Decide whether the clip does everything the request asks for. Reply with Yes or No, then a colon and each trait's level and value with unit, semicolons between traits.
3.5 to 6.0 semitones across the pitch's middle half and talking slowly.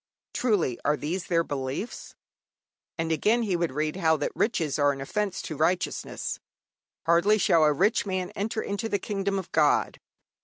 No: average, 4.9 semitones; average, 165 wpm